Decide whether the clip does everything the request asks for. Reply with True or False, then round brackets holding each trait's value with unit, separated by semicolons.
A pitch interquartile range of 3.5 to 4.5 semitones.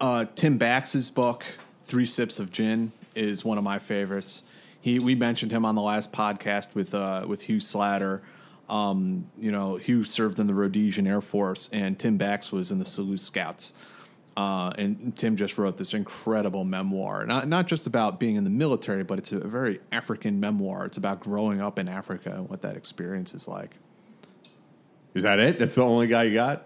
True (4.1 semitones)